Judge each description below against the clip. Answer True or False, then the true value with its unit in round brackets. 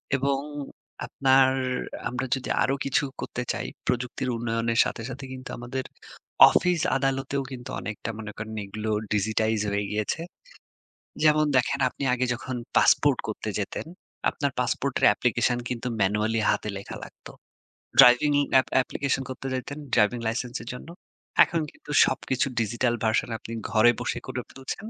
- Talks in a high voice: False (125 Hz)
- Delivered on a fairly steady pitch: False (3.3 semitones)